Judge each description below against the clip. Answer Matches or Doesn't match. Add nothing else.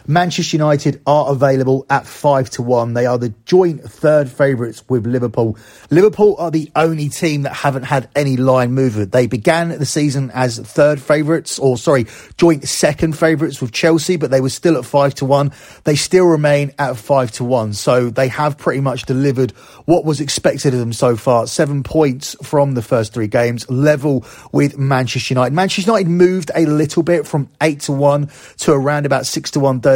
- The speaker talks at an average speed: Matches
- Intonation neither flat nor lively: Matches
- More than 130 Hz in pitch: Matches